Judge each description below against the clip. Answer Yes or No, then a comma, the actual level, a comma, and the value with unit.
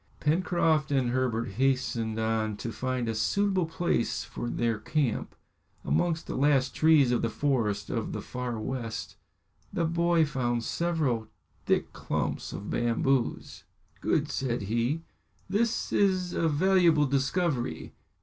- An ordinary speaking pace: No, slow, 130 wpm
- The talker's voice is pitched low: Yes, low, 130 Hz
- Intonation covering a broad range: Yes, wide, 5.7 semitones